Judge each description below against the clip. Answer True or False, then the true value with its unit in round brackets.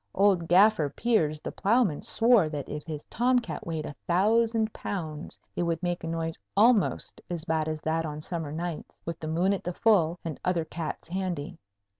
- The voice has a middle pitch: True (170 Hz)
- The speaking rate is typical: True (185 wpm)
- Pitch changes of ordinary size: True (4.0 semitones)